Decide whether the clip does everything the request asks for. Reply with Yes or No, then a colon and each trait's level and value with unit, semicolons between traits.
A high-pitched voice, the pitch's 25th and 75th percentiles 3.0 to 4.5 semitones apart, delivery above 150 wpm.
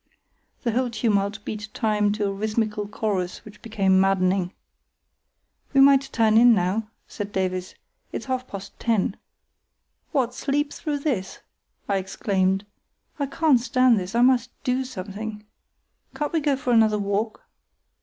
No: high, 215 Hz; average, 4.1 semitones; average, 145 wpm